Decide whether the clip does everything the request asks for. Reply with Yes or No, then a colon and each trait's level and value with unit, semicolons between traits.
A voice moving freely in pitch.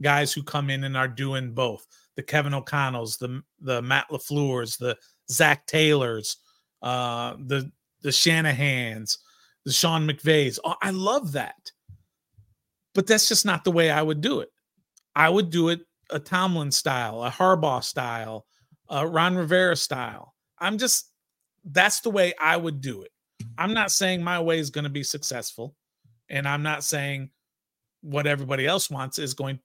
No: average, 4.4 semitones